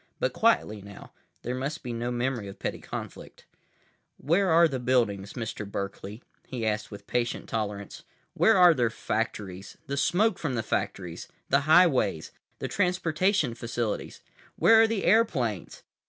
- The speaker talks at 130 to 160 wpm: Yes, average, 150 wpm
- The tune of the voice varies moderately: No, wide, 7.9 semitones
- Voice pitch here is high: No, low, 125 Hz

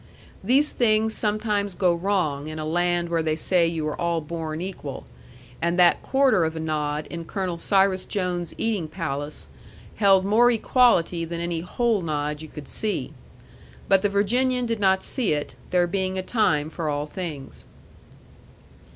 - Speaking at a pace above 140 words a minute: Yes, average, 165 wpm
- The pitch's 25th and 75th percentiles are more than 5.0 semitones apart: No, average, 4.3 semitones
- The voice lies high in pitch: No, medium, 175 Hz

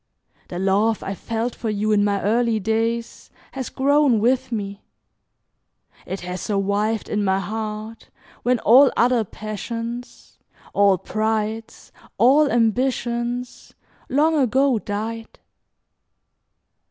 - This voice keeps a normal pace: No, slow, 110 wpm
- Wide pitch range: No, average, 2.8 semitones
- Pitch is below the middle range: No, high, 225 Hz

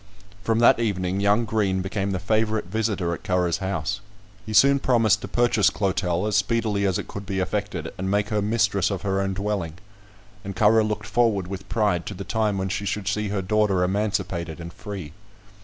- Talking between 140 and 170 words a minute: No, average, 195 wpm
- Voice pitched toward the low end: Yes, low, 100 Hz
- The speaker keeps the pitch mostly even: Yes, narrow, 2.2 semitones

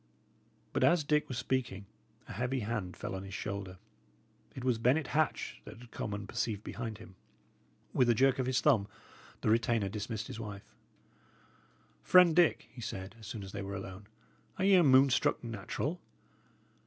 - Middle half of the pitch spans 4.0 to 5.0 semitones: Yes, average, 4.6 semitones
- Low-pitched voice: Yes, low, 115 Hz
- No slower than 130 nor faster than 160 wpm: No, average, 175 wpm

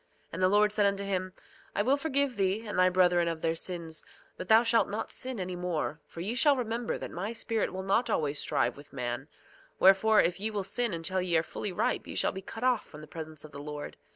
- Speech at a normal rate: No, fast, 240 wpm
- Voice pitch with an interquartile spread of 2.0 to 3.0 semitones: No, average, 4.9 semitones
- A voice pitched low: No, high, 190 Hz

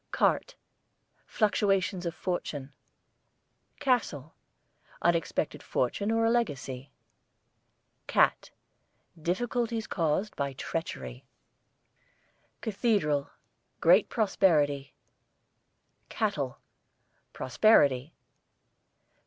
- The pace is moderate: No, slow, 60 wpm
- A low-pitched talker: No, medium, 170 Hz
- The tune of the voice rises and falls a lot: Yes, wide, 7.2 semitones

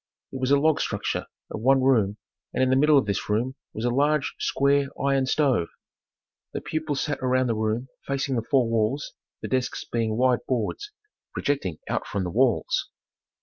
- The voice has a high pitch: No, low, 130 Hz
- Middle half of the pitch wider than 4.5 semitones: No, average, 3.4 semitones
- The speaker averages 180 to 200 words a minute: Yes, average, 185 wpm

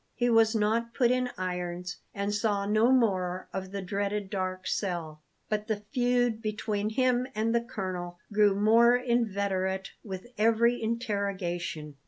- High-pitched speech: Yes, high, 210 Hz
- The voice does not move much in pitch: No, average, 3.7 semitones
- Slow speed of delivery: No, average, 145 wpm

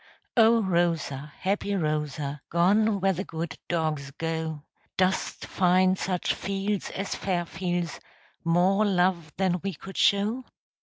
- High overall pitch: No, medium, 180 Hz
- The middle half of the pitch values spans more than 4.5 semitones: No, average, 3.2 semitones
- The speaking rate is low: Yes, slow, 120 wpm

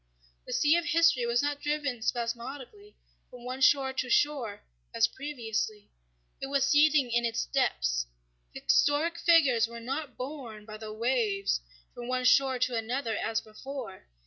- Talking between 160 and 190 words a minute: No, average, 145 wpm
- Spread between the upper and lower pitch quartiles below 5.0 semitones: Yes, average, 3.9 semitones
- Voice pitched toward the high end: Yes, very high, 255 Hz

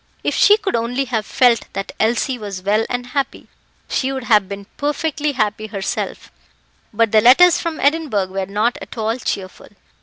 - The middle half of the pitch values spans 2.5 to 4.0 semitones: No, average, 4.7 semitones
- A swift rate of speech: No, average, 175 wpm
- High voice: Yes, high, 230 Hz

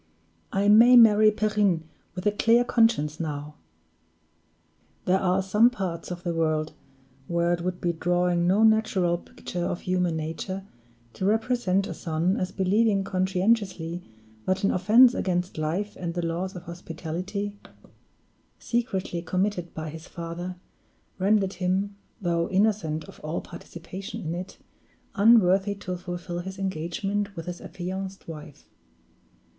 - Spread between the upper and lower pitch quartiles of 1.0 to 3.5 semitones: Yes, average, 2.8 semitones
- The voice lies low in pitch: No, medium, 185 Hz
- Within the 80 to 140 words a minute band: Yes, slow, 135 wpm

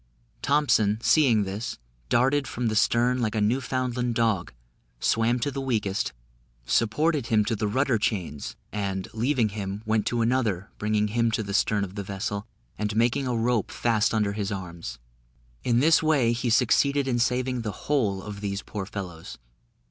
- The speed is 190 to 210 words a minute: No, average, 170 wpm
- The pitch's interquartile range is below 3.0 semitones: No, average, 3.3 semitones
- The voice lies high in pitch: No, low, 115 Hz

